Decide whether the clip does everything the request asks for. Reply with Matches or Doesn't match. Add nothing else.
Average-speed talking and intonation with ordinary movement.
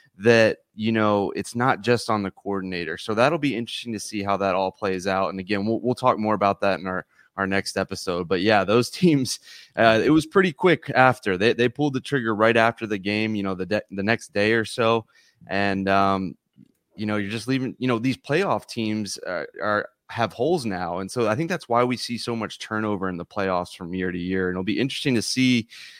Doesn't match